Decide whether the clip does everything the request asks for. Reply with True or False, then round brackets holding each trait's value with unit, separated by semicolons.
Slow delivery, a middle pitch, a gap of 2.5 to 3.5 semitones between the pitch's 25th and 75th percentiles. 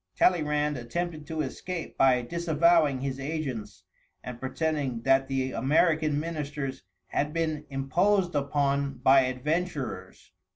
True (115 wpm; 145 Hz; 3.2 semitones)